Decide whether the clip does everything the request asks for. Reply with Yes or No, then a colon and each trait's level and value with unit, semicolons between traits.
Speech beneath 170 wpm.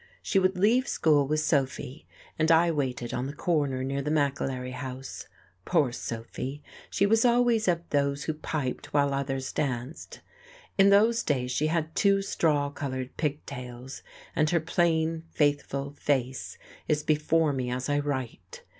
Yes: average, 155 wpm